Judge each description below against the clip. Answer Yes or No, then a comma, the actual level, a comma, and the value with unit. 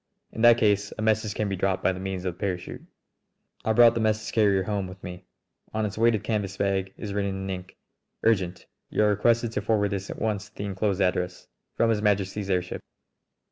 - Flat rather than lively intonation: Yes, narrow, 2.3 semitones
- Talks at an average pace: No, fast, 210 wpm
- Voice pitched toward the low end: Yes, low, 100 Hz